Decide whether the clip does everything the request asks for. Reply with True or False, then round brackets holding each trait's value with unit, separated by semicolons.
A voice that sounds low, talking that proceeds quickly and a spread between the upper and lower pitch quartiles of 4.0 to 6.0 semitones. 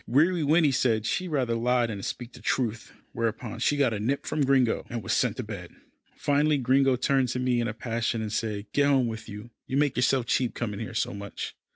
False (125 Hz; 225 wpm; 3.3 semitones)